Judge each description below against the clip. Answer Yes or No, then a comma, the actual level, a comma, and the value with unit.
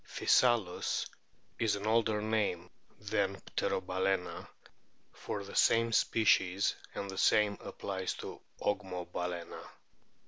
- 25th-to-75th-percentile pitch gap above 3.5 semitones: No, average, 2.8 semitones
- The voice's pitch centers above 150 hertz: No, low, 100 Hz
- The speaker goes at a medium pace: No, slow, 100 wpm